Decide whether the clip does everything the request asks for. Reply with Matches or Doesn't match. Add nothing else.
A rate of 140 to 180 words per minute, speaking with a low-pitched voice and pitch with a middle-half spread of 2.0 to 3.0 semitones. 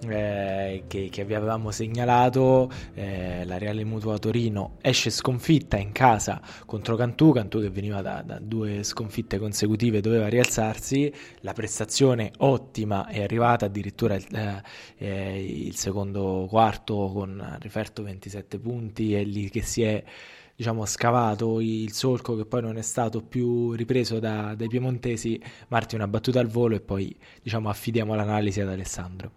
Matches